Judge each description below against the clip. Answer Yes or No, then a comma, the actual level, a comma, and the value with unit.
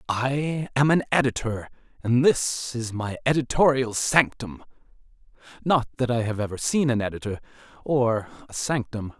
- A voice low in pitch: Yes, low, 125 Hz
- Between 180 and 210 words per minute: No, slow, 135 wpm